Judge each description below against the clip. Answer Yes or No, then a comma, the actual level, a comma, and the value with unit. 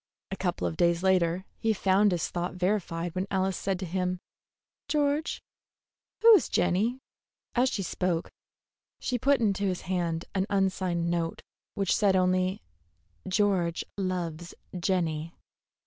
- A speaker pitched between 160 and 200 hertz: Yes, medium, 185 Hz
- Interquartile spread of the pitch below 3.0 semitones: Yes, narrow, 2.4 semitones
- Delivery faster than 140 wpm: No, slow, 135 wpm